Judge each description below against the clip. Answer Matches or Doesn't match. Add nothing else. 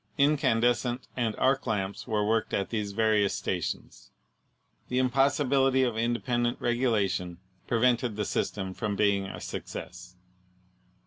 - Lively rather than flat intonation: Doesn't match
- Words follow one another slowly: Matches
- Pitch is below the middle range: Matches